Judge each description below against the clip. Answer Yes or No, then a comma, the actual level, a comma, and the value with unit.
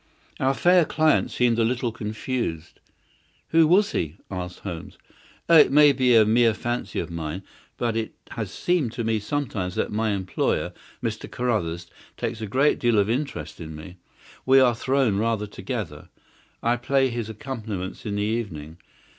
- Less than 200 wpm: Yes, average, 165 wpm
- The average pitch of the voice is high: No, low, 115 Hz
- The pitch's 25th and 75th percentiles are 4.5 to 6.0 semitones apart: Yes, average, 4.9 semitones